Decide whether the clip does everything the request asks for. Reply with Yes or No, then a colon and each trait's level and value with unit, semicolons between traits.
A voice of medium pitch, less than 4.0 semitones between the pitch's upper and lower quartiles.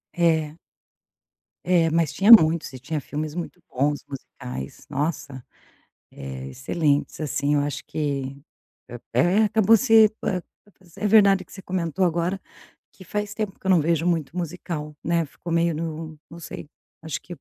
Yes: medium, 165 Hz; average, 3.5 semitones